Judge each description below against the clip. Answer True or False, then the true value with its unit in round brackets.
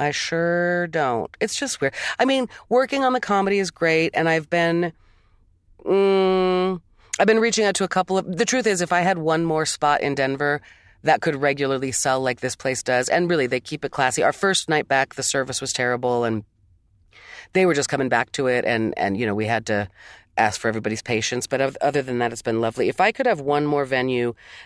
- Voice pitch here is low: False (145 Hz)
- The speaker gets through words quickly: True (230 wpm)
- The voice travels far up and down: True (6.8 semitones)